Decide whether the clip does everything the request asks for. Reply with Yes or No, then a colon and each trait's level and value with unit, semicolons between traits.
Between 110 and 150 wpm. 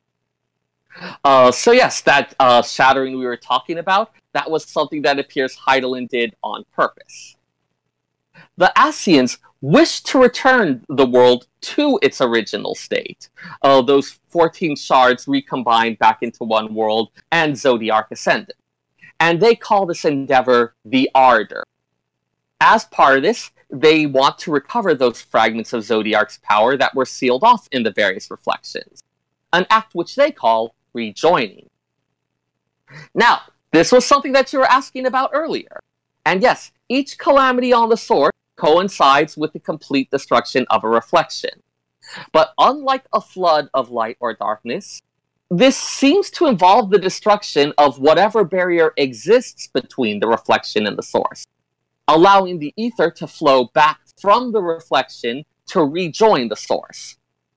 Yes: average, 145 wpm